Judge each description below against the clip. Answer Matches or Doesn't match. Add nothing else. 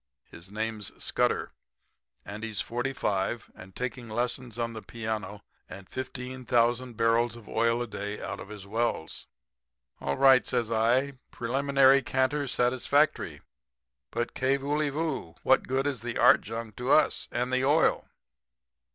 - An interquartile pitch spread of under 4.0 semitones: Matches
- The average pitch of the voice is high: Doesn't match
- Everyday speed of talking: Matches